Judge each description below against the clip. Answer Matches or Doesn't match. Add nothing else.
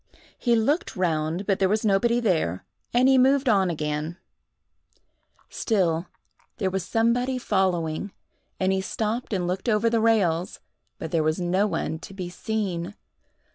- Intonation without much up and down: Doesn't match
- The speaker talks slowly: Doesn't match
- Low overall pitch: Doesn't match